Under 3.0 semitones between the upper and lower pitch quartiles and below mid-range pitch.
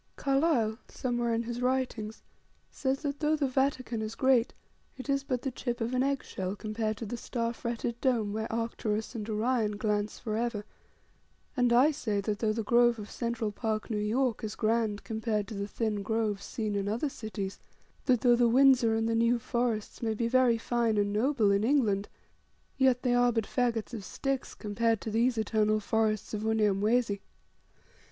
No: narrow, 2.6 semitones; high, 230 Hz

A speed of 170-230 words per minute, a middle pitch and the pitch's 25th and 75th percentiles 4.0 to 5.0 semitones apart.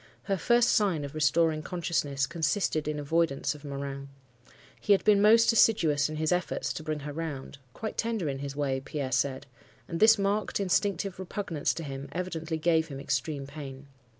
Yes: average, 180 wpm; medium, 155 Hz; average, 4.7 semitones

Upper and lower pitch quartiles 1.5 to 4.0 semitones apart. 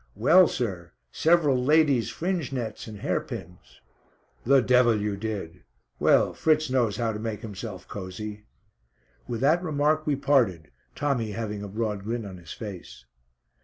No: average, 5.2 semitones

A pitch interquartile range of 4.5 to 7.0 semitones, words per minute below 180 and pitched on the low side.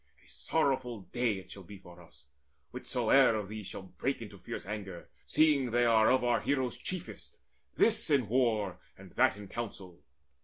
Yes: average, 4.9 semitones; average, 170 wpm; low, 115 Hz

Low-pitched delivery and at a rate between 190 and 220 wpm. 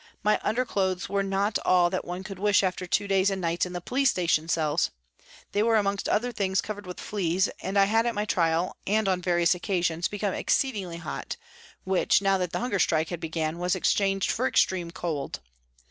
No: high, 190 Hz; average, 200 wpm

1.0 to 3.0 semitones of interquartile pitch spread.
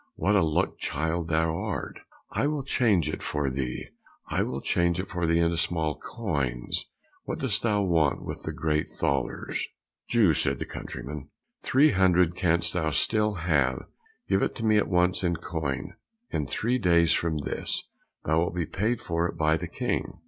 No: average, 3.7 semitones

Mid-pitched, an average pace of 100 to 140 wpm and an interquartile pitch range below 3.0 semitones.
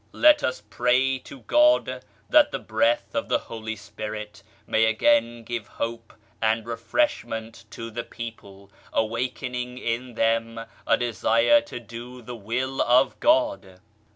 No: low, 115 Hz; slow, 135 wpm; narrow, 2.4 semitones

